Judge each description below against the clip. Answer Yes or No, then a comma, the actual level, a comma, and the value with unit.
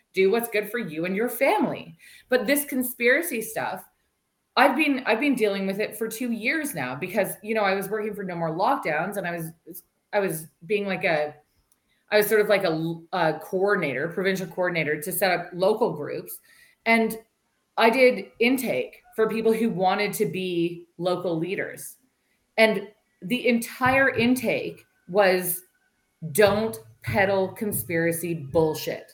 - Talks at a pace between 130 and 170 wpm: Yes, average, 150 wpm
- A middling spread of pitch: Yes, average, 4.6 semitones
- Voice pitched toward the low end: No, high, 205 Hz